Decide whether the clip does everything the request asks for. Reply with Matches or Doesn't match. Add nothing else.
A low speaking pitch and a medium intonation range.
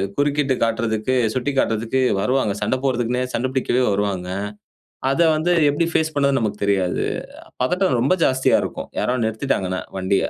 Matches